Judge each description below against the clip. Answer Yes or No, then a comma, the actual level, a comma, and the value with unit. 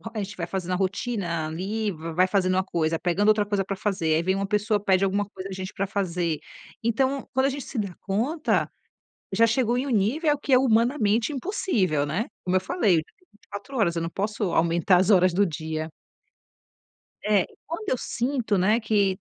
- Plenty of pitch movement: No, average, 3.9 semitones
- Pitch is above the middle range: Yes, high, 200 Hz